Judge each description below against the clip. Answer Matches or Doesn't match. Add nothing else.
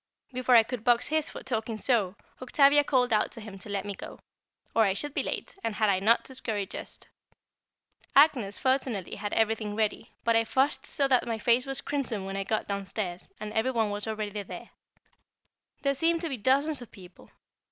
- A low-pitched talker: Doesn't match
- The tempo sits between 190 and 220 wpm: Matches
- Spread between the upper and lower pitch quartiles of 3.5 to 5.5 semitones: Matches